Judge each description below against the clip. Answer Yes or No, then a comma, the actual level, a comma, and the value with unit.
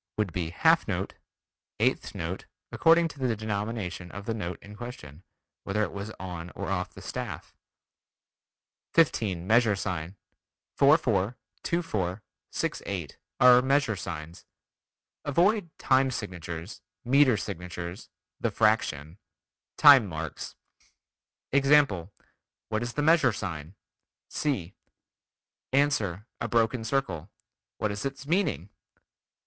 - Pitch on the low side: Yes, low, 105 Hz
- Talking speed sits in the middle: No, slow, 120 wpm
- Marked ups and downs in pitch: Yes, wide, 6.8 semitones